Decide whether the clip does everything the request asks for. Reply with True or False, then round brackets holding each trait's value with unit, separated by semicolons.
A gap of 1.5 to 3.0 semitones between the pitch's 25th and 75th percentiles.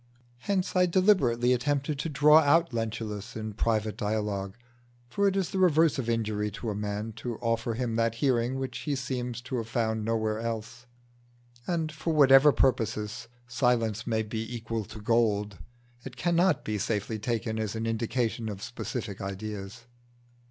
False (3.5 semitones)